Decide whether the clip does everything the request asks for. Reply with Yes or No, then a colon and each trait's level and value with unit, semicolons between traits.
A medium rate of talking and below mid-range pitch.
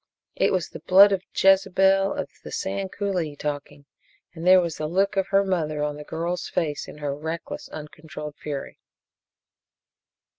No: average, 160 wpm; medium, 170 Hz